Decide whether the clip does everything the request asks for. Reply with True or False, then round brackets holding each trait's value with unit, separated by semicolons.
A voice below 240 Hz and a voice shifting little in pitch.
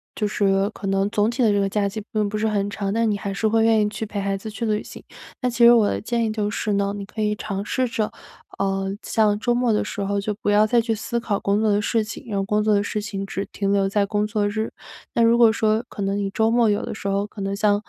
True (210 Hz; 1.7 semitones)